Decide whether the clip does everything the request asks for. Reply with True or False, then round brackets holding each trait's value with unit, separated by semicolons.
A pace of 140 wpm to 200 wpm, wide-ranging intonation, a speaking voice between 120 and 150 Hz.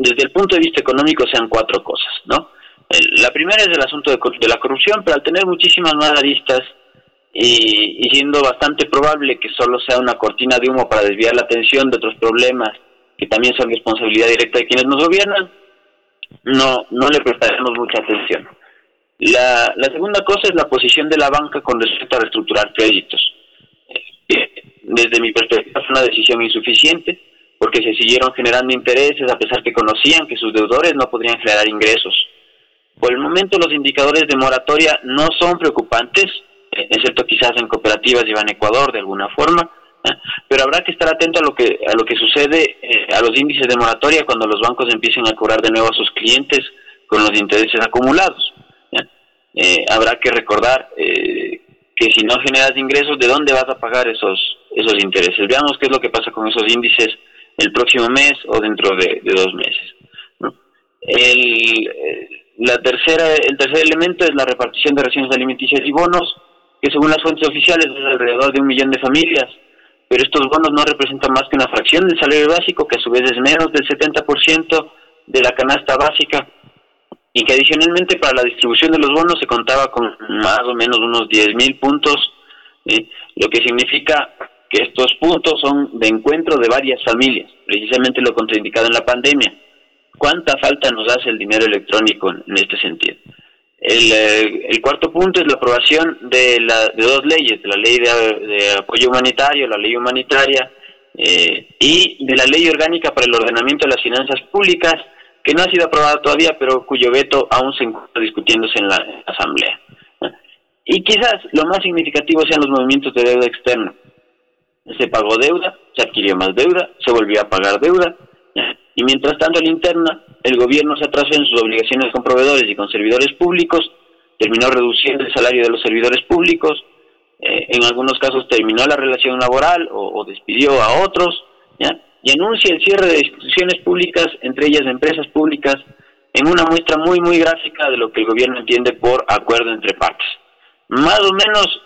True (185 wpm; 5.7 semitones; 140 Hz)